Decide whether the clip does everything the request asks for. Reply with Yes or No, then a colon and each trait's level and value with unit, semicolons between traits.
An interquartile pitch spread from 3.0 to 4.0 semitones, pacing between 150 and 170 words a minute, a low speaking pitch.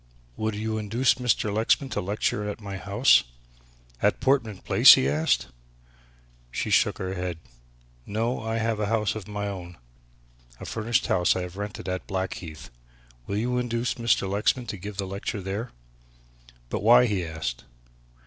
Yes: average, 3.3 semitones; average, 160 wpm; low, 105 Hz